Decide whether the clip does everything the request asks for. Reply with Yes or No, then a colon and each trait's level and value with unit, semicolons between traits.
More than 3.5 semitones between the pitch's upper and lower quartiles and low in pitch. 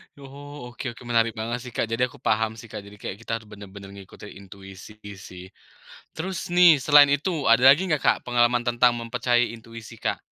Yes: average, 4.0 semitones; low, 120 Hz